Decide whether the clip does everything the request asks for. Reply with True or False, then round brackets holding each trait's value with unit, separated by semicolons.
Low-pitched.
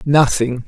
True (130 Hz)